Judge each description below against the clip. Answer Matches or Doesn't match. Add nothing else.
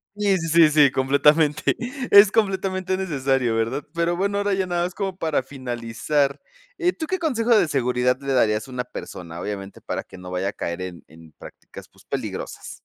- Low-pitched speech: Doesn't match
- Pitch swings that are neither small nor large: Doesn't match